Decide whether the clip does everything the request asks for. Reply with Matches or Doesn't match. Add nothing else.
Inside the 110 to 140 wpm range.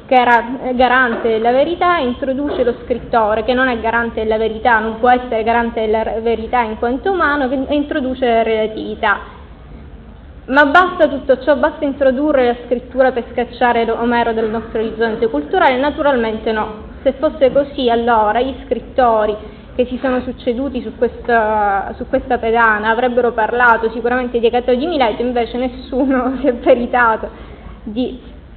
Doesn't match